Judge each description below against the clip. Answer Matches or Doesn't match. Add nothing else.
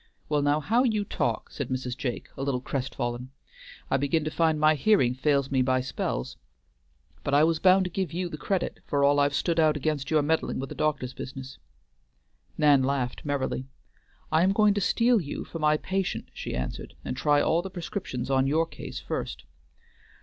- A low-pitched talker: Doesn't match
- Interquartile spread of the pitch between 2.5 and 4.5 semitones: Matches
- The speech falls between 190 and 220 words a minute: Matches